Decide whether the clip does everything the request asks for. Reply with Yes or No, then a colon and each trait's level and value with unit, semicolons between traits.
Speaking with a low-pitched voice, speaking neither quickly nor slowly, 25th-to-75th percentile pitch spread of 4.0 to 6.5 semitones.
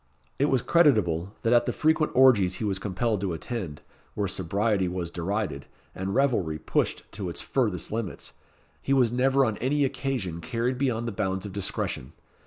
Yes: low, 105 Hz; average, 175 wpm; wide, 5.4 semitones